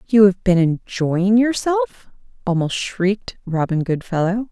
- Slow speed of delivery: Yes, slow, 120 wpm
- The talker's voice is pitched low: No, high, 195 Hz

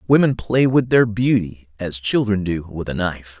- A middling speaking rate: Yes, average, 195 wpm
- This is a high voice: No, low, 105 Hz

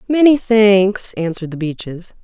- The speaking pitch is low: No, high, 200 Hz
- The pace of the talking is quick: No, slow, 135 wpm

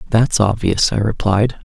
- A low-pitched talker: Yes, low, 105 Hz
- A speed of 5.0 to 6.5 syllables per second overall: No, 4.1 syllables/s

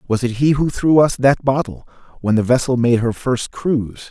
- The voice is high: No, low, 125 Hz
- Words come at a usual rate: No, fast, 220 wpm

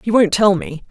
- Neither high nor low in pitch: No, high, 200 Hz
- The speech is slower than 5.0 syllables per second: No, 5.2 syllables/s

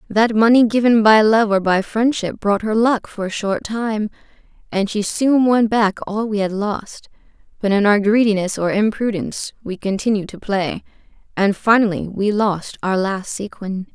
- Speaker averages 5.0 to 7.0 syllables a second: No, 4.5 syllables/s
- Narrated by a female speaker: Yes, female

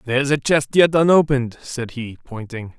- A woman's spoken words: No, male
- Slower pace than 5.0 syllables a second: No, 5.5 syllables/s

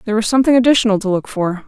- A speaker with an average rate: No, fast, 250 wpm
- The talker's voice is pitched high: Yes, high, 215 Hz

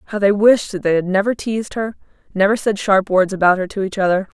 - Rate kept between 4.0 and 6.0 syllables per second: No, 6.2 syllables/s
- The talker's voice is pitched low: No, high, 200 Hz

